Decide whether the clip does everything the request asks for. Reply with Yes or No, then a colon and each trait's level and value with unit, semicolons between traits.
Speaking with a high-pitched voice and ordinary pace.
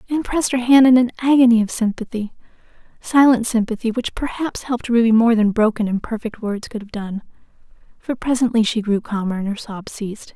Yes: high, 230 Hz; average, 180 wpm